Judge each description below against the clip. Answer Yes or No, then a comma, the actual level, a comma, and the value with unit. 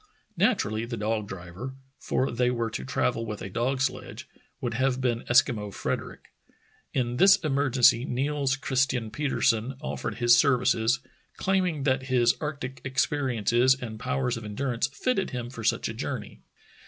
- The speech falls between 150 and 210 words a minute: Yes, average, 160 wpm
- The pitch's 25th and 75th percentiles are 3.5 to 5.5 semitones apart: No, average, 2.8 semitones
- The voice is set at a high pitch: No, low, 125 Hz